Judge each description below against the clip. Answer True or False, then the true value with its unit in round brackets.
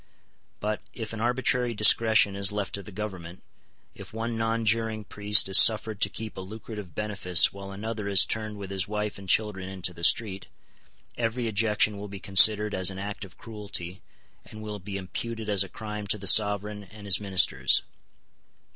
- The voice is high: False (105 Hz)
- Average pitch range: False (2.0 semitones)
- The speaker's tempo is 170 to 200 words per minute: True (180 wpm)